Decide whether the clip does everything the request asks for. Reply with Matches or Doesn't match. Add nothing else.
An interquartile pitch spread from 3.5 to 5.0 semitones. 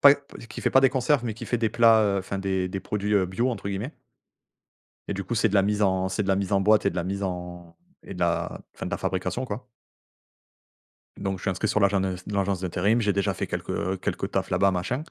Doesn't match